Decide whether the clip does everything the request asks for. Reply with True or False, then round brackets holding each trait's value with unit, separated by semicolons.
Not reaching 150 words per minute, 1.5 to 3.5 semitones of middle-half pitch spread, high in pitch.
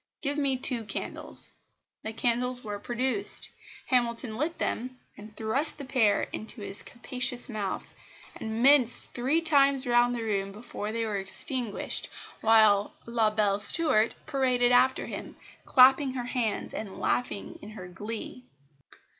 True (140 wpm; 3.2 semitones; 240 Hz)